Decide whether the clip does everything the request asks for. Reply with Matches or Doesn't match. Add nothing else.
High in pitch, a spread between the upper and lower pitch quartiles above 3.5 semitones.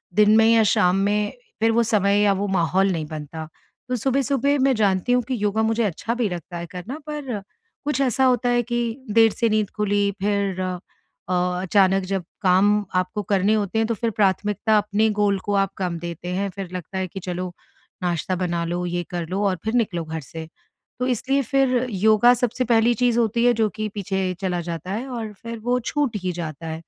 Matches